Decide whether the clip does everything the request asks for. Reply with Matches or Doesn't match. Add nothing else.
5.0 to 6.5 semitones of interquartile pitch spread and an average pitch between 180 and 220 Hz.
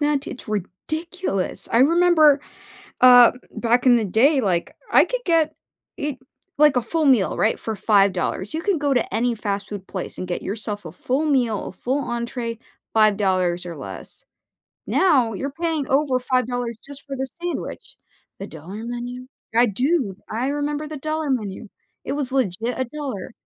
Doesn't match